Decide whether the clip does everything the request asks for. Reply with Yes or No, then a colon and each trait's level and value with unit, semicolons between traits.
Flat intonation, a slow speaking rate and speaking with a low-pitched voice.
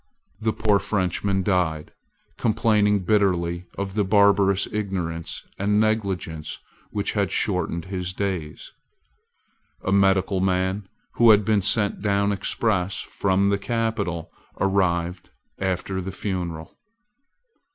Yes: narrow, 2.1 semitones; slow, 110 wpm; very low, 95 Hz